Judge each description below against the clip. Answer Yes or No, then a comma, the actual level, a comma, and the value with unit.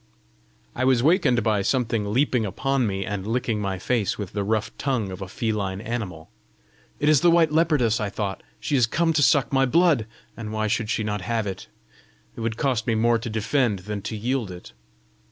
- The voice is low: Yes, low, 115 Hz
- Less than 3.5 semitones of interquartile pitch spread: No, average, 4.1 semitones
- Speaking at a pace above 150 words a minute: Yes, fast, 205 wpm